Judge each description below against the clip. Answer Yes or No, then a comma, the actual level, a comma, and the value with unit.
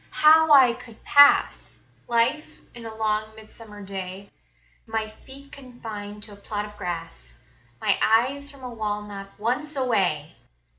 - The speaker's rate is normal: Yes, average, 145 wpm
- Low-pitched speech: No, high, 220 Hz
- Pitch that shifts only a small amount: No, average, 3.6 semitones